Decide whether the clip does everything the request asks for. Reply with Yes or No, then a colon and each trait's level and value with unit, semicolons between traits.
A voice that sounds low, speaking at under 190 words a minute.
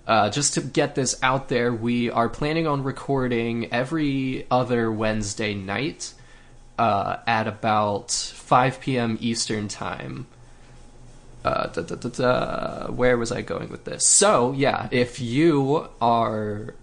Yes: low, 120 Hz; average, 140 wpm